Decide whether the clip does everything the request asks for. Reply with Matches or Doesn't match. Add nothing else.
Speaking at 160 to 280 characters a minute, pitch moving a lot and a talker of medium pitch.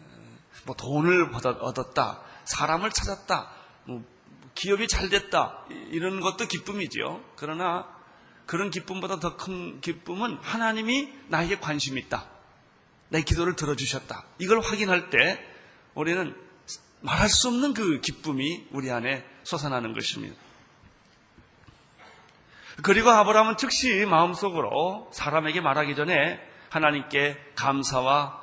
Matches